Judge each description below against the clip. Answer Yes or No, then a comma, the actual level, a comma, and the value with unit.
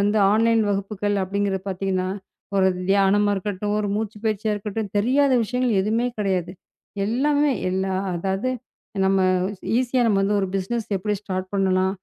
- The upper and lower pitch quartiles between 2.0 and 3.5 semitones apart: Yes, narrow, 2.4 semitones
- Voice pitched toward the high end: Yes, high, 205 Hz